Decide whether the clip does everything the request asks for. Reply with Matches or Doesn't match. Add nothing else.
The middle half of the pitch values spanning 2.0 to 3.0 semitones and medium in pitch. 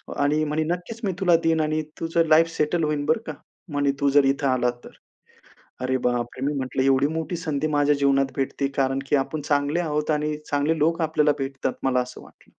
Matches